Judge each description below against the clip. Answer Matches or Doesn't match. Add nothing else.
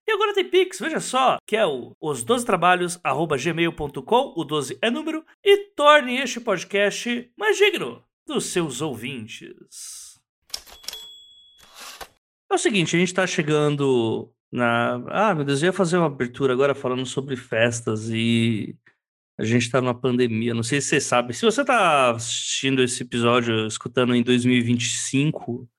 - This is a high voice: Doesn't match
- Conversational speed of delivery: Matches